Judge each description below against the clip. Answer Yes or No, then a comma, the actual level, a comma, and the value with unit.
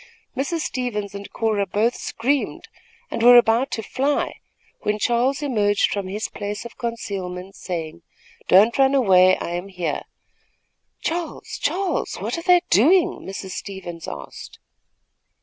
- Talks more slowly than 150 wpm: Yes, slow, 135 wpm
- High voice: Yes, high, 215 Hz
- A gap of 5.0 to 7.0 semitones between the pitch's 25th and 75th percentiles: Yes, wide, 5.4 semitones